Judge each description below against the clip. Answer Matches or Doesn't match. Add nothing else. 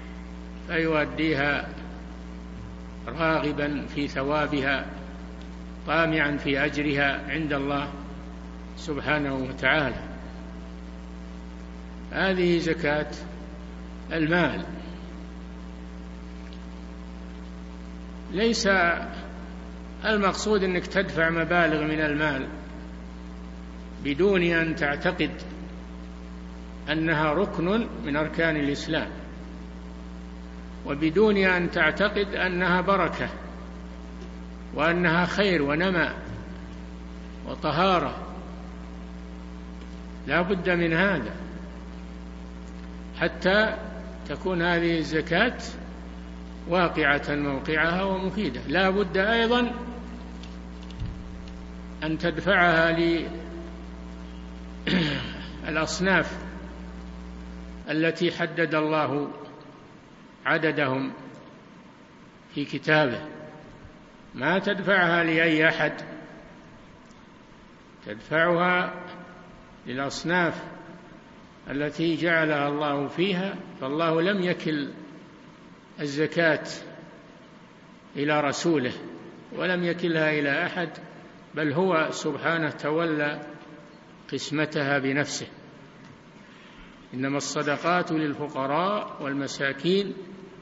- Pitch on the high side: Doesn't match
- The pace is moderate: Doesn't match